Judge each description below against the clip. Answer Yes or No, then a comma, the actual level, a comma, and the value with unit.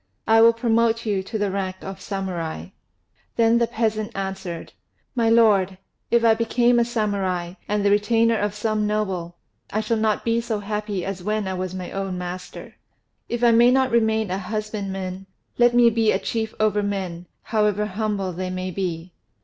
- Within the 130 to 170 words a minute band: No, average, 180 wpm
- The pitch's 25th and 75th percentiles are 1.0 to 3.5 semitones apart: Yes, average, 3.1 semitones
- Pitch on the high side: Yes, high, 210 Hz